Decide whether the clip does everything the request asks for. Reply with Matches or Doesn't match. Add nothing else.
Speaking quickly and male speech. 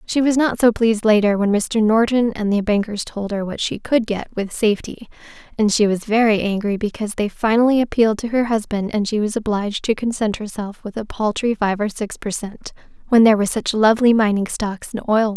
Doesn't match